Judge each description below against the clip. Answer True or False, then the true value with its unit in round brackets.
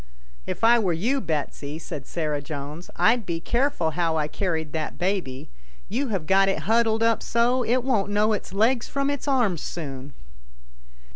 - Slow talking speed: False (185 wpm)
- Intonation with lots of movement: True (6.7 semitones)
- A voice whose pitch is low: False (195 Hz)